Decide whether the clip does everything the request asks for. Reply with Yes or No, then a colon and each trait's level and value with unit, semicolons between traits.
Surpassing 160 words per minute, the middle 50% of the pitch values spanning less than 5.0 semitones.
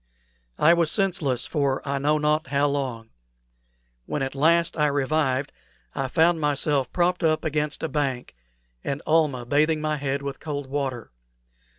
No: average, 155 wpm; narrow, 2.4 semitones